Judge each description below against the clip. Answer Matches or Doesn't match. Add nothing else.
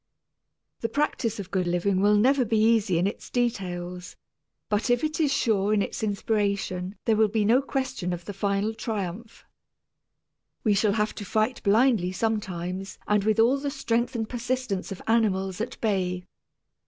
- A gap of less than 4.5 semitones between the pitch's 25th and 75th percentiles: Matches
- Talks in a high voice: Matches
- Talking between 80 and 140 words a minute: Doesn't match